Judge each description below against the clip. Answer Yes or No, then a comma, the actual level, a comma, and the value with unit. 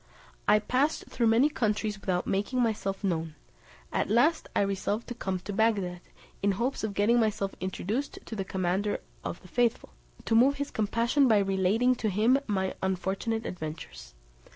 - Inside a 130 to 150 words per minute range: No, average, 165 wpm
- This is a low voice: No, high, 210 Hz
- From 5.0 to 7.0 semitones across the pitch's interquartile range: No, average, 3.6 semitones